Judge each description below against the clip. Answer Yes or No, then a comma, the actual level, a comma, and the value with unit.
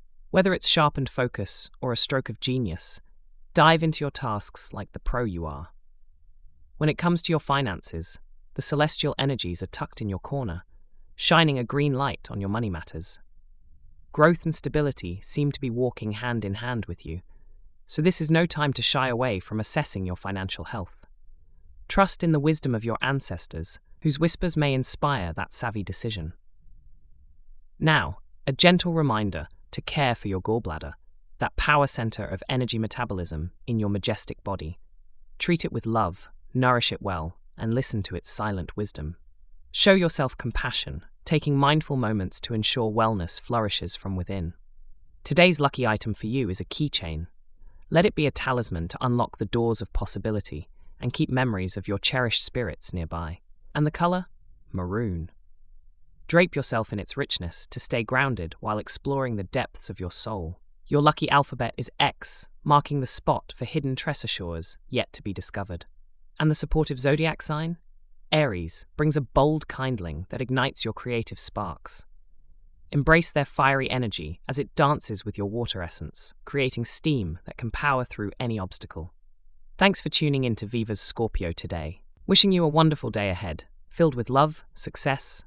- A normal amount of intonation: No, wide, 8.3 semitones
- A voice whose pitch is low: Yes, low, 110 Hz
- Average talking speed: Yes, average, 165 wpm